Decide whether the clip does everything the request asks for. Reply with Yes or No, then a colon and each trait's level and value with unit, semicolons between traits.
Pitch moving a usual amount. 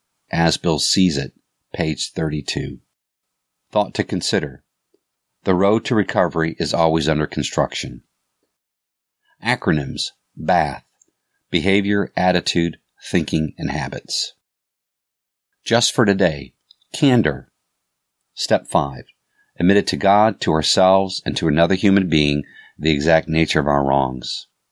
Yes: average, 4.3 semitones